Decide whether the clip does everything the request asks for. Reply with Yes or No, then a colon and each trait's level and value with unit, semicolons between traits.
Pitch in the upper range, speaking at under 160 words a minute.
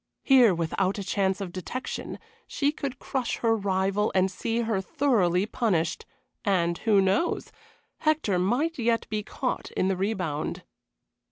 Yes: high, 205 Hz; average, 145 wpm